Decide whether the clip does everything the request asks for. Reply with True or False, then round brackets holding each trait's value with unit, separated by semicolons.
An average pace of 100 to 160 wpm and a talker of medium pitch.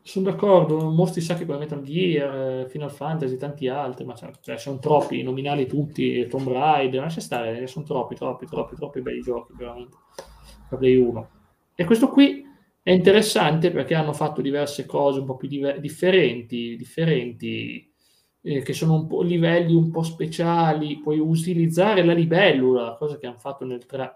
False (170 wpm; 145 Hz)